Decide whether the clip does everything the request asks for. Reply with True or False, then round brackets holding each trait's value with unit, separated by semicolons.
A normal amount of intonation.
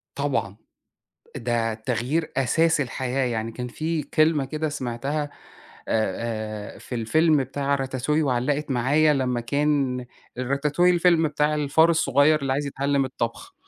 True (3.6 semitones)